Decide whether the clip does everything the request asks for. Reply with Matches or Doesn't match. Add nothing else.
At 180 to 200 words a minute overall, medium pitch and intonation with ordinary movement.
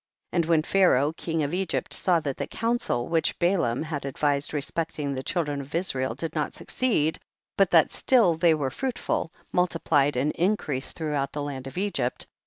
Matches